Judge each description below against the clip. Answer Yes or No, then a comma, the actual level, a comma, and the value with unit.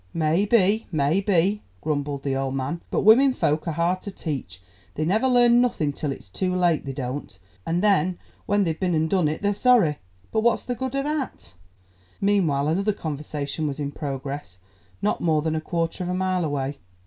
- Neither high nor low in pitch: Yes, medium, 165 Hz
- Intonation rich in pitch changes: Yes, wide, 5.7 semitones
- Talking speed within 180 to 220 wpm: Yes, average, 195 wpm